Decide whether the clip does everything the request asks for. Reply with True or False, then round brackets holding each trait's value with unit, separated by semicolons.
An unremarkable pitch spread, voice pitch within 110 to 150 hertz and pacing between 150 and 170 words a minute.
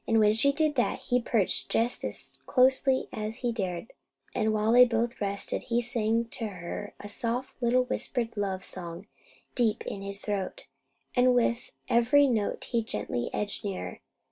False (3.3 semitones; 225 Hz; 165 wpm)